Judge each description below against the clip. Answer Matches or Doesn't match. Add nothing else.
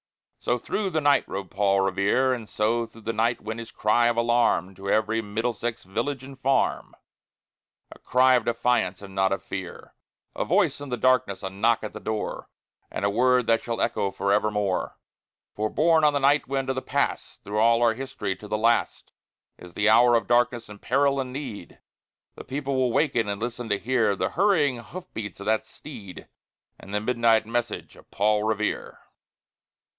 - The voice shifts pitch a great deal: Doesn't match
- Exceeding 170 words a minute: Matches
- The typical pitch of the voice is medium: Doesn't match